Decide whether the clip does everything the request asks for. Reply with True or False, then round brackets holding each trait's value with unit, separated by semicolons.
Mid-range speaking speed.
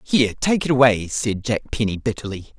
True (185 wpm)